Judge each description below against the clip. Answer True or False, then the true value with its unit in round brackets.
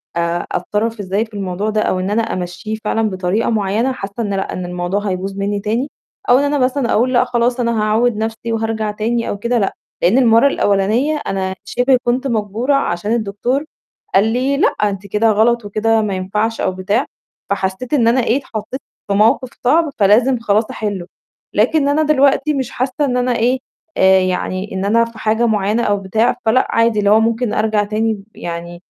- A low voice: False (220 Hz)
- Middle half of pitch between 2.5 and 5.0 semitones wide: True (3.4 semitones)